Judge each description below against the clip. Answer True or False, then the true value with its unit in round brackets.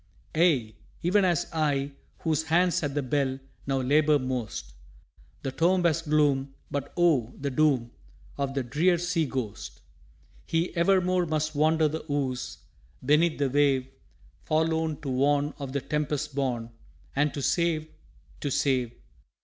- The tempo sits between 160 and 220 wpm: False (140 wpm)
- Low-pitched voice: False (145 Hz)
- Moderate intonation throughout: True (3.1 semitones)